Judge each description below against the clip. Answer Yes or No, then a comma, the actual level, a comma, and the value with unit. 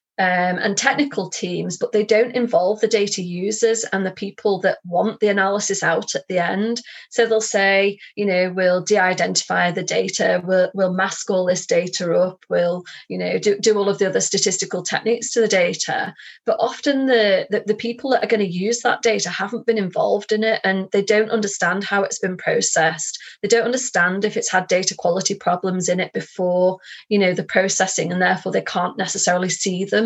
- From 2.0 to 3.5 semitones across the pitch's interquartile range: Yes, average, 2.9 semitones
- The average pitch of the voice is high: Yes, high, 195 Hz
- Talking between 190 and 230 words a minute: Yes, fast, 205 wpm